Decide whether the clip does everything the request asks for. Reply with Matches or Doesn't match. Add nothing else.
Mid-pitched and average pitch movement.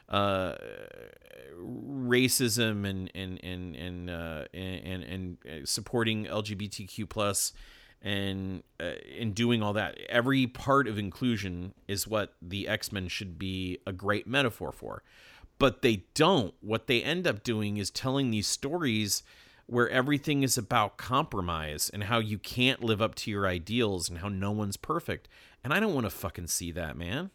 Doesn't match